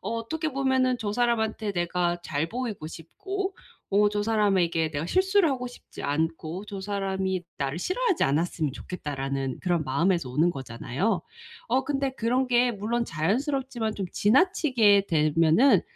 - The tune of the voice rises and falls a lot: Yes, wide, 7.3 semitones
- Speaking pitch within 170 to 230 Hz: Yes, high, 205 Hz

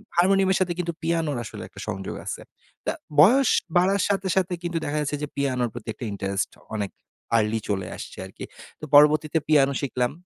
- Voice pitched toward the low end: No, medium, 150 Hz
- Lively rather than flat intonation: Yes, wide, 6.5 semitones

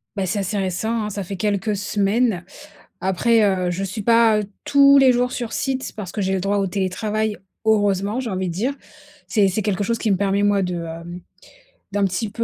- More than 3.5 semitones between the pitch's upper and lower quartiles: No, average, 2.7 semitones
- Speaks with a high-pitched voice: Yes, high, 205 Hz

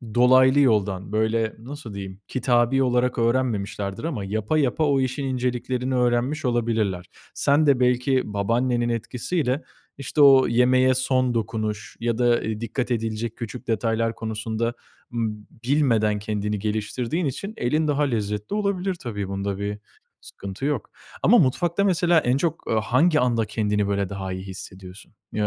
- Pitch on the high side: No, low, 120 Hz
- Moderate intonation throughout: Yes, average, 3.7 semitones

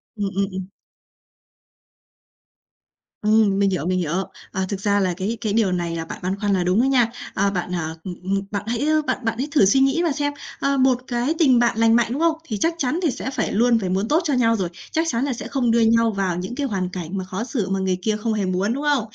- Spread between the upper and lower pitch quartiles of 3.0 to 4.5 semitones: No, average, 4.9 semitones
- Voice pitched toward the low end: No, high, 215 Hz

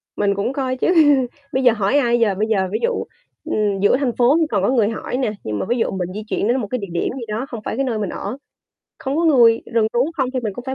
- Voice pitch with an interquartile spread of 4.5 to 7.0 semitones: No, average, 3.8 semitones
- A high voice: Yes, high, 235 Hz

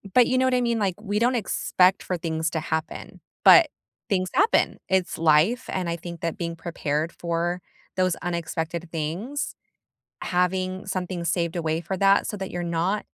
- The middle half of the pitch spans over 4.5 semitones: No, narrow, 2.6 semitones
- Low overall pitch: No, medium, 175 Hz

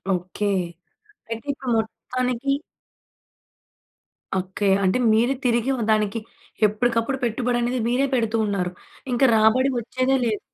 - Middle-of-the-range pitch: No, high, 230 Hz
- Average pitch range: Yes, average, 3.0 semitones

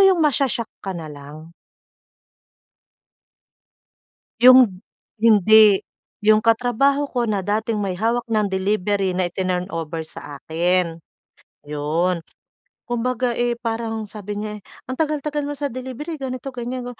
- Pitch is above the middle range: Yes, high, 220 Hz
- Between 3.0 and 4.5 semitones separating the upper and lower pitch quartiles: No, wide, 5.4 semitones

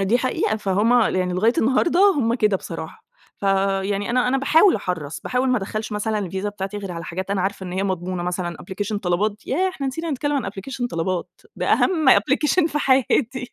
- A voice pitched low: No, high, 210 Hz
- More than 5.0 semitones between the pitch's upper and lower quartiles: Yes, wide, 5.4 semitones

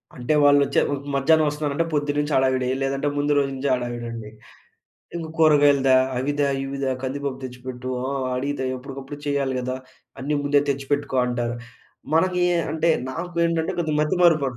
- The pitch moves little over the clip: Yes, narrow, 2.3 semitones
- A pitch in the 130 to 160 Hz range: Yes, medium, 140 Hz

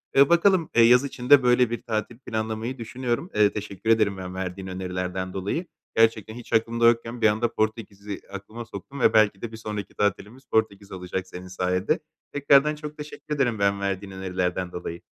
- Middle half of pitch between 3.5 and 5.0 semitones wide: Yes, average, 4.1 semitones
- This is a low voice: Yes, low, 110 Hz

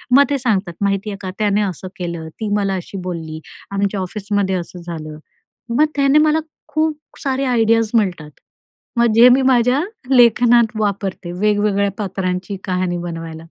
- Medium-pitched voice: No, high, 200 Hz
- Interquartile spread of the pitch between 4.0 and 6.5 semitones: Yes, average, 4.5 semitones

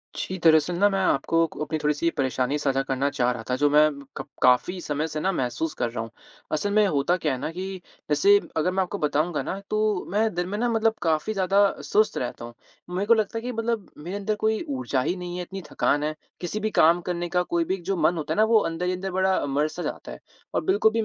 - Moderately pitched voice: Yes, medium, 175 Hz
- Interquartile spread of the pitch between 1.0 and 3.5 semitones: No, average, 5.0 semitones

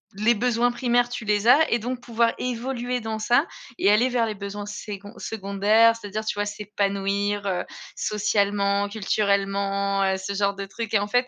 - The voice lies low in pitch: No, high, 210 Hz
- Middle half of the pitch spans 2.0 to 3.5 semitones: Yes, average, 2.8 semitones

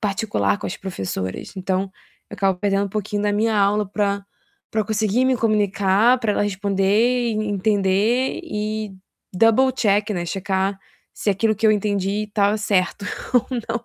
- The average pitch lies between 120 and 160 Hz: No, high, 205 Hz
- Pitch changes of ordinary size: No, narrow, 2.0 semitones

